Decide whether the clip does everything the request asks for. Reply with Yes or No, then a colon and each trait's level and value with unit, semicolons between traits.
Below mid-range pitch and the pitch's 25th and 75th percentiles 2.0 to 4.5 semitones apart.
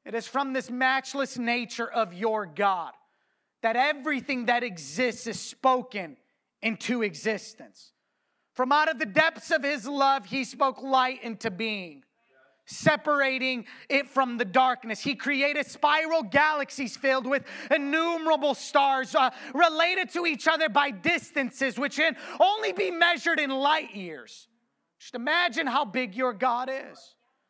No: very high, 270 Hz; average, 3.8 semitones